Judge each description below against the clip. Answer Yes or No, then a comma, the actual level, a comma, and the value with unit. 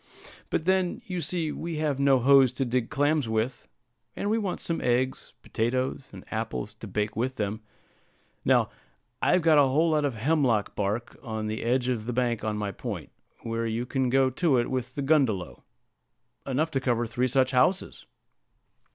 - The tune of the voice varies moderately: Yes, average, 4.1 semitones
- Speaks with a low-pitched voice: Yes, low, 130 Hz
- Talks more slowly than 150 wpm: No, average, 180 wpm